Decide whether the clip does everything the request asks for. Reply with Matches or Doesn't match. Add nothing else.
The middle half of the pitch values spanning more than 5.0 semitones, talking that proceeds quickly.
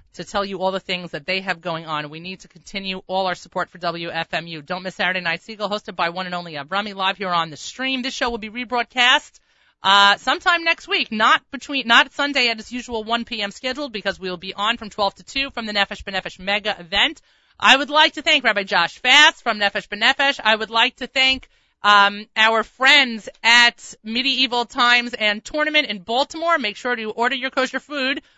Matches